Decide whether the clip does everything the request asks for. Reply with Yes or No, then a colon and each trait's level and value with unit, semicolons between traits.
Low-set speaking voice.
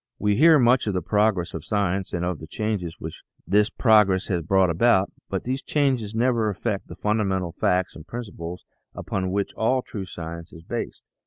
Yes: low, 100 Hz